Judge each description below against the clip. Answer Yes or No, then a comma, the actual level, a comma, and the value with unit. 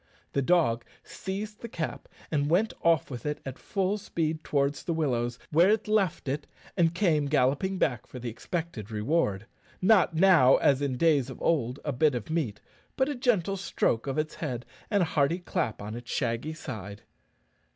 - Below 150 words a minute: No, average, 180 wpm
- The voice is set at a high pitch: No, medium, 150 Hz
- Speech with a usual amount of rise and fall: No, wide, 5.8 semitones